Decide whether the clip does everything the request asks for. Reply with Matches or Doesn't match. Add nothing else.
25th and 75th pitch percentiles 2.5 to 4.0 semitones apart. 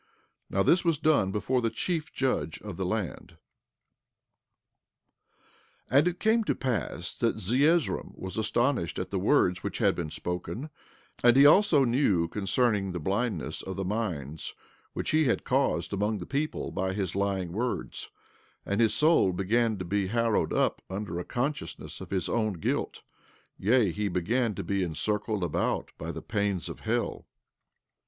Doesn't match